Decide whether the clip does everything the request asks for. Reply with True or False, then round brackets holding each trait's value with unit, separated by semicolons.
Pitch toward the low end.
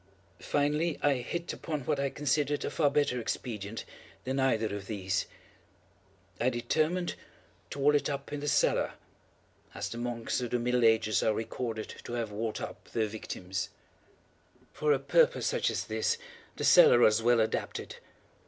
True (125 Hz)